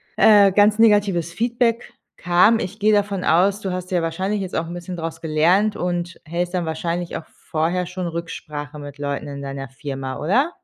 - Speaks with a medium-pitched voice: Yes, medium, 175 Hz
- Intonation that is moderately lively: Yes, average, 3.9 semitones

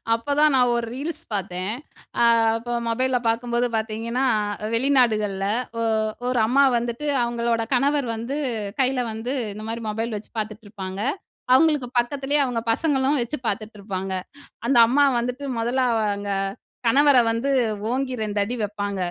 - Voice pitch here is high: Yes, high, 235 Hz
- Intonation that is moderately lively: Yes, average, 3.4 semitones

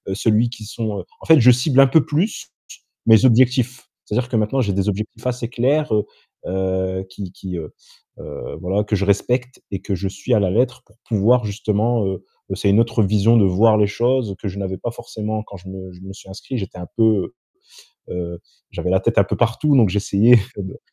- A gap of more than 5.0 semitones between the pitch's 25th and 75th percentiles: No, average, 3.8 semitones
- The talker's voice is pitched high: No, low, 105 Hz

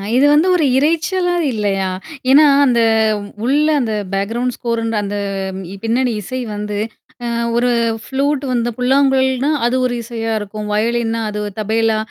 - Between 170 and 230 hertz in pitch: No, high, 240 Hz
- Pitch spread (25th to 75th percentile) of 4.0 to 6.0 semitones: No, average, 3.4 semitones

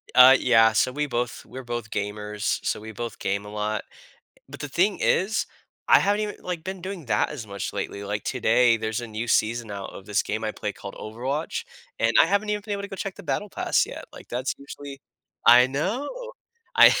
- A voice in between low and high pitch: No, low, 120 Hz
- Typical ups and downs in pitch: No, wide, 7.8 semitones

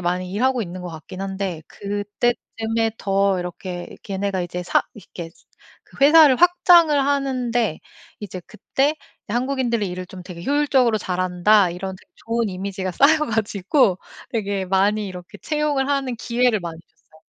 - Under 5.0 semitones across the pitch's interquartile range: No, wide, 5.5 semitones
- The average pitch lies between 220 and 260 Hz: No, high, 205 Hz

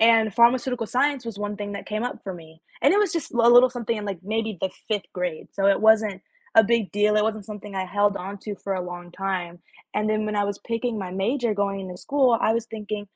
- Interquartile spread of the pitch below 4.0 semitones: Yes, average, 2.8 semitones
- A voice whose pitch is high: Yes, high, 210 Hz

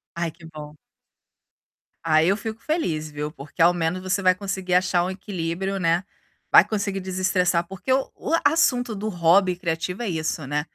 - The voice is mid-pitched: Yes, medium, 180 Hz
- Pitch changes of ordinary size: Yes, average, 3.1 semitones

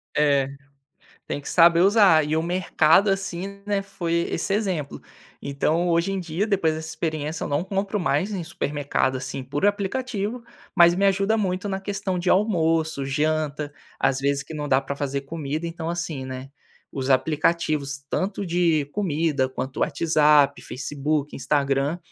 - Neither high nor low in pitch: Yes, medium, 160 Hz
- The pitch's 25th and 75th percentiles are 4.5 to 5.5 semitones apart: Yes, average, 4.9 semitones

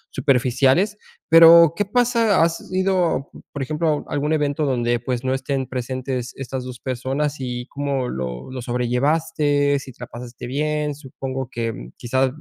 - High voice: No, low, 135 Hz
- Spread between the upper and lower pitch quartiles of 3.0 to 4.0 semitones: Yes, average, 3.3 semitones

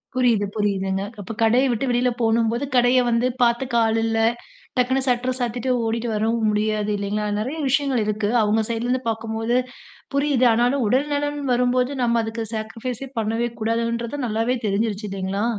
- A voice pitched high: Yes, high, 230 Hz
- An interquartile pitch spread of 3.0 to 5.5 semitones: No, narrow, 2.4 semitones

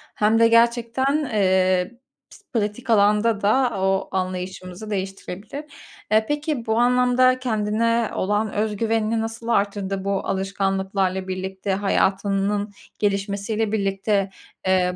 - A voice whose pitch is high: Yes, high, 205 Hz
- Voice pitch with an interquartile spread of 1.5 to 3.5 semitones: Yes, average, 3.0 semitones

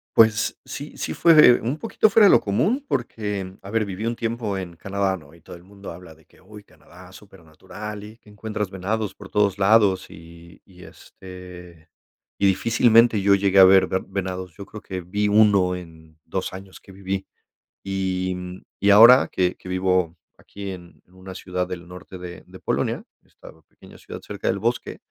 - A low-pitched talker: Yes, very low, 95 Hz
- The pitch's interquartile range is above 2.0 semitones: Yes, narrow, 2.5 semitones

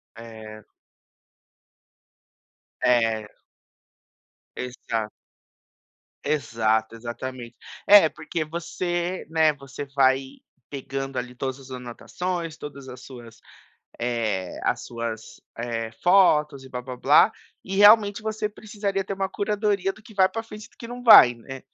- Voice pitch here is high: No, low, 135 Hz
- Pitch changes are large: Yes, wide, 8.1 semitones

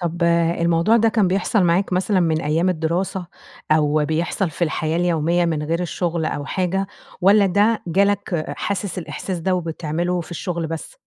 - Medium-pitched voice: Yes, medium, 175 Hz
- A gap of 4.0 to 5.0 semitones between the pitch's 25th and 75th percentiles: No, average, 2.8 semitones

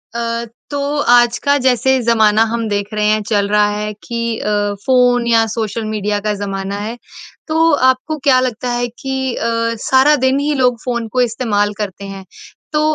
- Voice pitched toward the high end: Yes, high, 235 Hz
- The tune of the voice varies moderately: Yes, average, 3.6 semitones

